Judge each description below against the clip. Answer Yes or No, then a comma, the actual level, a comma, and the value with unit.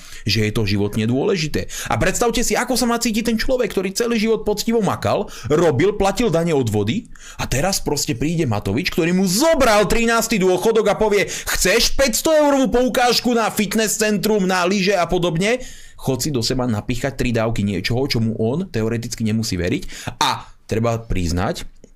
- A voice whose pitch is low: No, medium, 180 Hz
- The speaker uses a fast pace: Yes, fast, 175 wpm